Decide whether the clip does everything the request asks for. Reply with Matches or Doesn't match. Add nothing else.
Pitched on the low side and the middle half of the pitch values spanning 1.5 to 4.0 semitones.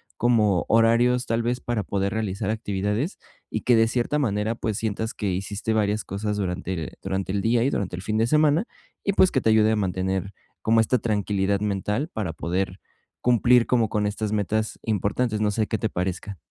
Matches